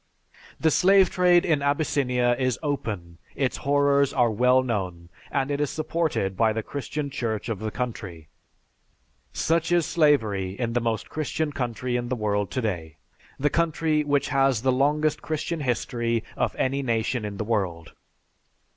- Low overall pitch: Yes, low, 130 Hz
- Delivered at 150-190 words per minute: Yes, average, 155 wpm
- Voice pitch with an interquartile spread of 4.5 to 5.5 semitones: Yes, average, 4.9 semitones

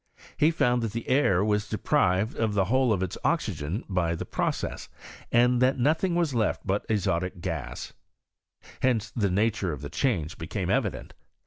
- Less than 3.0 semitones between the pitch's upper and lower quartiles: No, average, 4.9 semitones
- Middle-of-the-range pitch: No, low, 110 Hz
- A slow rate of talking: No, average, 175 wpm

